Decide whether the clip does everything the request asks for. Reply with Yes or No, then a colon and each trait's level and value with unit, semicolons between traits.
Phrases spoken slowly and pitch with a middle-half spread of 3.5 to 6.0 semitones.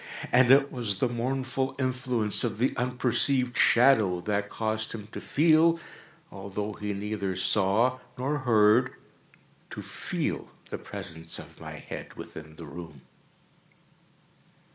Yes: slow, 120 wpm; average, 4.3 semitones